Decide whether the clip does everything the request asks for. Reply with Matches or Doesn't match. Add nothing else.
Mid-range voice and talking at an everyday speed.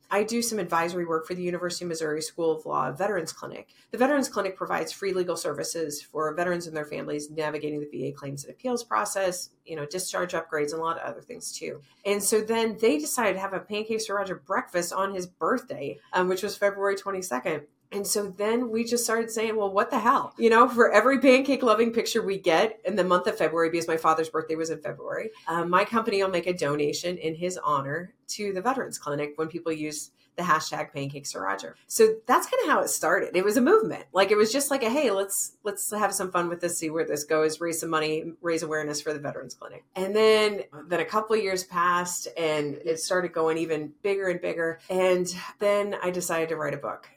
Doesn't match